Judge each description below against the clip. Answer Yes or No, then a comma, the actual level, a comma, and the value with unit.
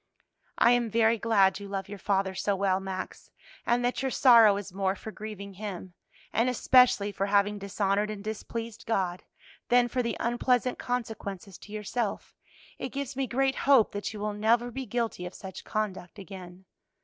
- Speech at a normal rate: Yes, average, 175 wpm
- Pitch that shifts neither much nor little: Yes, average, 3.3 semitones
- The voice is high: Yes, high, 210 Hz